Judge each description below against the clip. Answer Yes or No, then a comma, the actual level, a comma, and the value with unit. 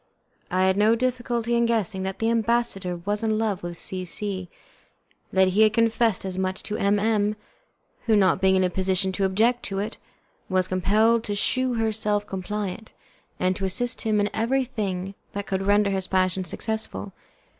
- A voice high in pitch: Yes, high, 205 Hz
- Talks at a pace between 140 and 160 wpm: No, average, 180 wpm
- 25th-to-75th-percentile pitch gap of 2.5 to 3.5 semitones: Yes, average, 2.9 semitones